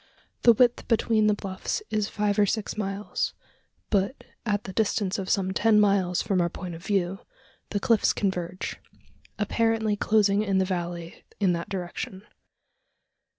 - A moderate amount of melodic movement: No, narrow, 2.2 semitones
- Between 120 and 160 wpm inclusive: Yes, average, 150 wpm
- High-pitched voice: Yes, high, 200 Hz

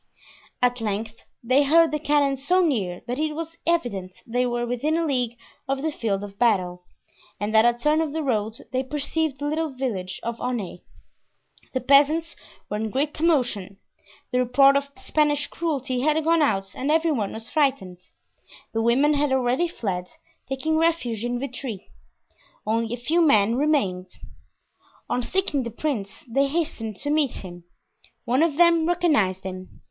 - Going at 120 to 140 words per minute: No, average, 165 wpm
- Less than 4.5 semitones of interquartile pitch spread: No, average, 5.3 semitones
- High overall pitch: Yes, very high, 260 Hz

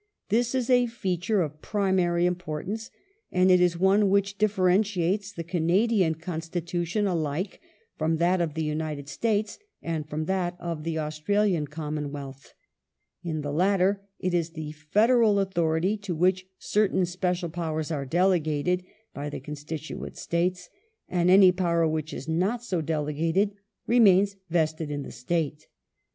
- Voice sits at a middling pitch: Yes, medium, 175 Hz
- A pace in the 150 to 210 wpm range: No, average, 140 wpm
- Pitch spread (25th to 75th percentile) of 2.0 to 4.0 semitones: Yes, average, 3.5 semitones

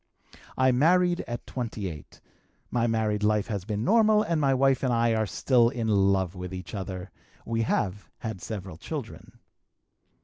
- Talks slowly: No, average, 160 wpm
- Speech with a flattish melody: No, average, 4.7 semitones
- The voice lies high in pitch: No, low, 110 Hz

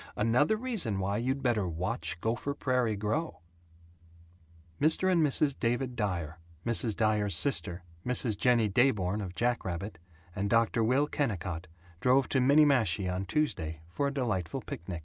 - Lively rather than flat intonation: Yes, wide, 6.2 semitones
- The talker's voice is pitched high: No, low, 115 Hz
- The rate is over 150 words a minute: No, average, 140 wpm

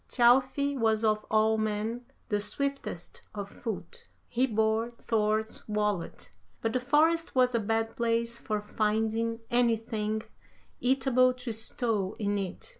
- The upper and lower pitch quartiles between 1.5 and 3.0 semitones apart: Yes, narrow, 2.5 semitones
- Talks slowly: Yes, slow, 130 wpm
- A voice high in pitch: Yes, high, 225 Hz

